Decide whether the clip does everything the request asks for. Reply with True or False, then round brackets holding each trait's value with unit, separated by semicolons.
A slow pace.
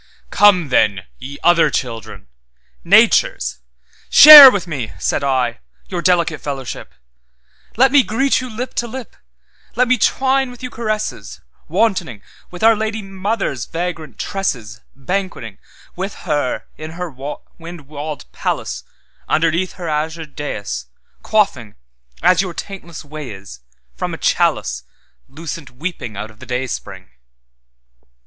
True (105 wpm)